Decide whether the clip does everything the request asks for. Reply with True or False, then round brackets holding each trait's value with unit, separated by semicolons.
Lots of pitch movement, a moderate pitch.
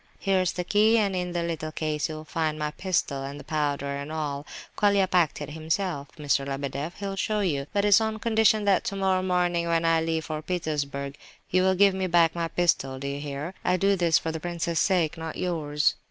False (3.8 semitones; 165 Hz)